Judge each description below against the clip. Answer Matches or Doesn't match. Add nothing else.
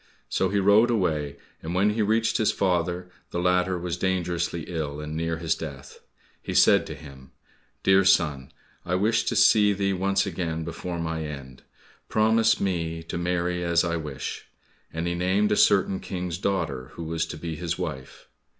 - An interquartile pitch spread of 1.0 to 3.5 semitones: Matches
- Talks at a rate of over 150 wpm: Matches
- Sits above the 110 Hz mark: Doesn't match